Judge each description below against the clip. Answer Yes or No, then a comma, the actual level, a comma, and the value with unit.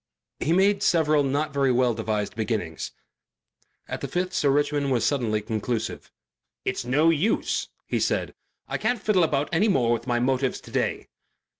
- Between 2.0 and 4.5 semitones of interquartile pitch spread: No, average, 5.2 semitones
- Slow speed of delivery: No, average, 165 wpm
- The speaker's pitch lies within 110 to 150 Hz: Yes, medium, 140 Hz